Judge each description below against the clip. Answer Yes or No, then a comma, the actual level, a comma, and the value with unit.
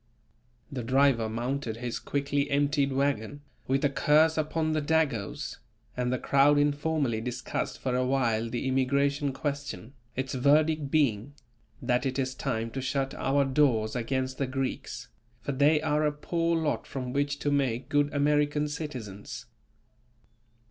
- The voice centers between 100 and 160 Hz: Yes, medium, 140 Hz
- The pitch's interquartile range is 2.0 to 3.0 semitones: Yes, narrow, 2.5 semitones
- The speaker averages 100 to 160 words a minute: Yes, average, 150 wpm